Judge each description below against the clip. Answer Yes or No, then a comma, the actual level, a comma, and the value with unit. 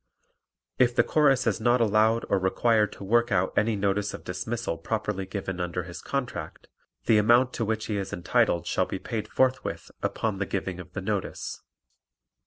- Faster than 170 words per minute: Yes, average, 180 wpm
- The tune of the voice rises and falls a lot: No, average, 3.5 semitones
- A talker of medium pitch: No, low, 105 Hz